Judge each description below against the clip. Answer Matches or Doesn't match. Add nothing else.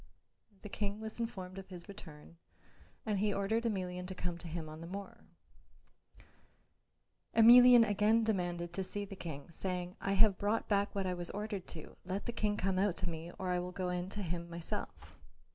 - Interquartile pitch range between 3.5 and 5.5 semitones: Doesn't match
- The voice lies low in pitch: Doesn't match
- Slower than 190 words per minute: Doesn't match